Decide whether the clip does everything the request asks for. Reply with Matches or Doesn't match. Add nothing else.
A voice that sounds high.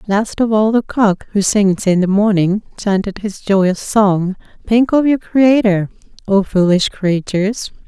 Matches